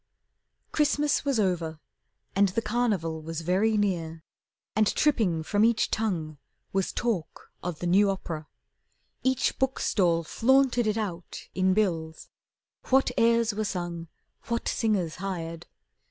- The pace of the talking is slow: Yes, slow, 130 wpm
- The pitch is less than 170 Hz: No, high, 195 Hz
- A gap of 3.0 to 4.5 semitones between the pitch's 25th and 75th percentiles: No, wide, 5.4 semitones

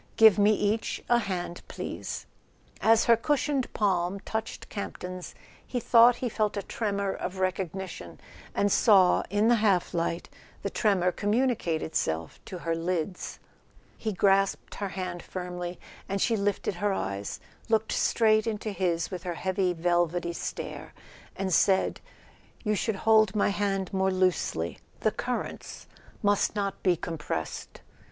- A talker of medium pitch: No, high, 195 Hz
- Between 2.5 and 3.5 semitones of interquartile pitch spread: Yes, average, 3.2 semitones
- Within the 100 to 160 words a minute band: Yes, average, 145 wpm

